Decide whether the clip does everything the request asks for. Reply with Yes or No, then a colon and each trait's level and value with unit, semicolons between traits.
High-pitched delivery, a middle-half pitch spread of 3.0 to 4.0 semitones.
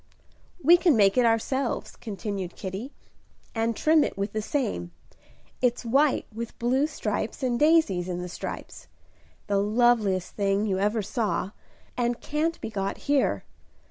No: high, 225 Hz; average, 4.9 semitones